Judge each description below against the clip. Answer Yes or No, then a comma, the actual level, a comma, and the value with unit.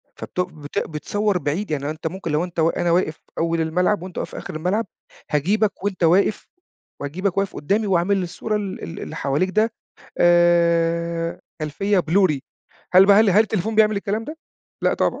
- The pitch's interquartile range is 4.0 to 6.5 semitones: No, average, 3.5 semitones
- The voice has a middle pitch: Yes, medium, 180 Hz